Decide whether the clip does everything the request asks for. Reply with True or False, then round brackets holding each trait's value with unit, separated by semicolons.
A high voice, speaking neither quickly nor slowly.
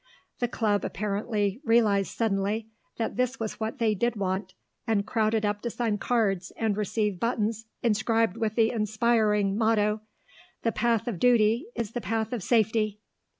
True (220 Hz; 155 wpm)